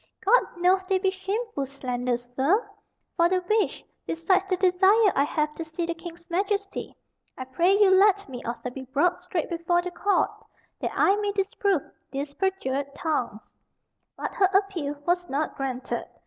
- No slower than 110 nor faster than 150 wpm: No, average, 165 wpm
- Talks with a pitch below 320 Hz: No, very high, 350 Hz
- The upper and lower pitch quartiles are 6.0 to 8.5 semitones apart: No, wide, 5.5 semitones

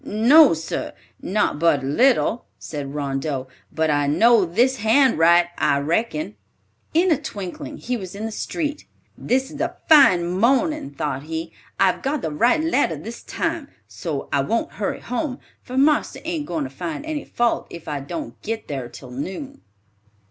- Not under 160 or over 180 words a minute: Yes, average, 170 wpm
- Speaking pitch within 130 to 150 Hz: No, high, 195 Hz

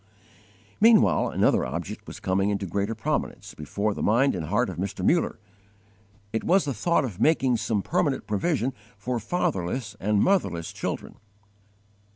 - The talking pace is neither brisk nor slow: Yes, average, 150 wpm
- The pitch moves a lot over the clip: Yes, wide, 5.9 semitones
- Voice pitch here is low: Yes, low, 110 Hz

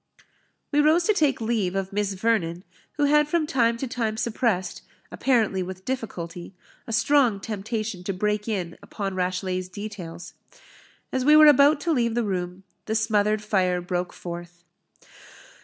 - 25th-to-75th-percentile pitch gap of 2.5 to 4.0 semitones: No, average, 4.8 semitones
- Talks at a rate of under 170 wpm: Yes, average, 155 wpm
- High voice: Yes, high, 210 Hz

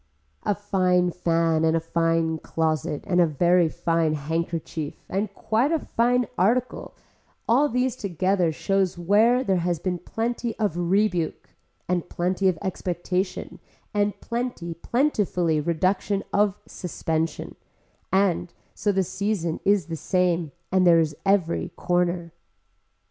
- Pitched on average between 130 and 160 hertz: No, medium, 180 Hz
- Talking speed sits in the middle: No, slow, 130 wpm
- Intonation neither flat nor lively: Yes, average, 3.5 semitones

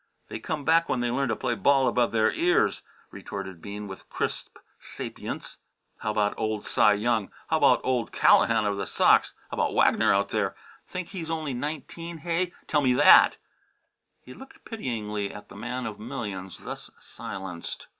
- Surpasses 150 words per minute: Yes, average, 175 wpm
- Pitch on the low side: Yes, low, 115 Hz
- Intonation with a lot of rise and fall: Yes, wide, 5.8 semitones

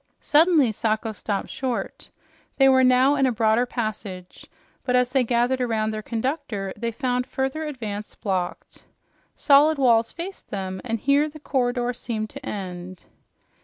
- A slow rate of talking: No, average, 150 wpm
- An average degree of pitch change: Yes, average, 3.6 semitones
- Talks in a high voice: Yes, high, 245 Hz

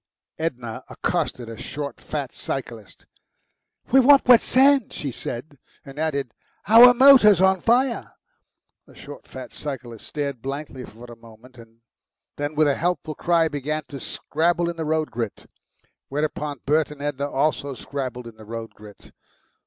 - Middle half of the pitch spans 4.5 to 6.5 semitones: Yes, average, 4.9 semitones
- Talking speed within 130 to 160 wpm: Yes, average, 150 wpm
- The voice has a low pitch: No, medium, 145 Hz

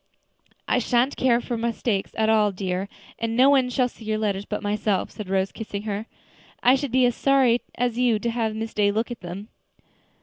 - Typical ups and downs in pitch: Yes, average, 3.0 semitones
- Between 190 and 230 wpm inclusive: Yes, fast, 205 wpm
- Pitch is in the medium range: No, high, 225 Hz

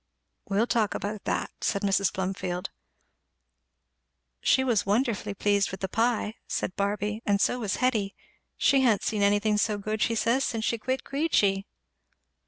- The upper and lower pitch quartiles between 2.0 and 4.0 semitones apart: Yes, narrow, 2.6 semitones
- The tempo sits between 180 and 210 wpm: No, average, 155 wpm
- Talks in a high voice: Yes, high, 210 Hz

